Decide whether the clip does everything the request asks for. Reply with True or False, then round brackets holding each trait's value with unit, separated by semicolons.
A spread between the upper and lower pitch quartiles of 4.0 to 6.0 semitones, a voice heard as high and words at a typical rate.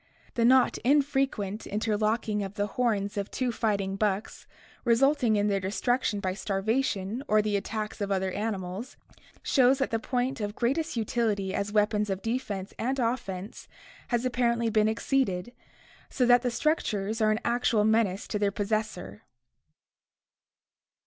False (3.3 semitones; 215 Hz; 145 wpm)